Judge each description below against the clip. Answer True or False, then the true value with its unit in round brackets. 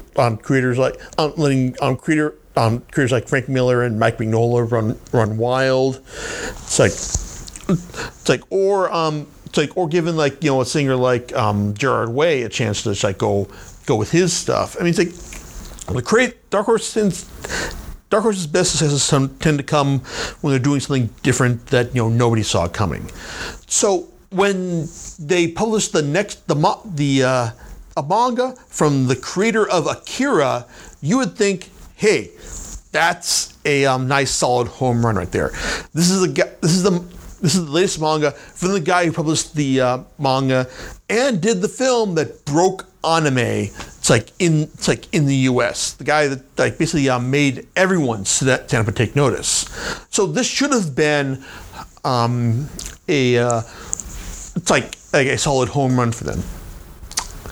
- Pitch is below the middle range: False (145 Hz)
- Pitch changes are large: True (5.9 semitones)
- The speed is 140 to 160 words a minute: False (170 wpm)